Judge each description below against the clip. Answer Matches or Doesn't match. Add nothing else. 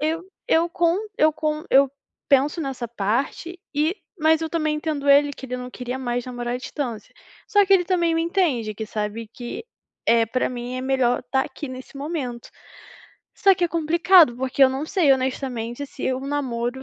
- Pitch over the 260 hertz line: Matches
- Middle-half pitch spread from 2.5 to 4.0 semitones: Doesn't match